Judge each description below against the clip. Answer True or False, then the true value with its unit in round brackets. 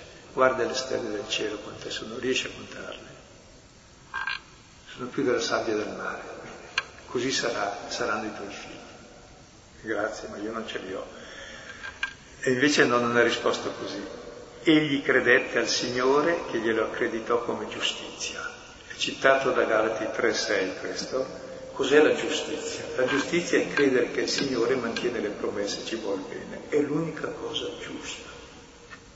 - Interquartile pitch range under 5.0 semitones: True (4.0 semitones)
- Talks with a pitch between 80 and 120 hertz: False (140 Hz)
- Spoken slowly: False (145 wpm)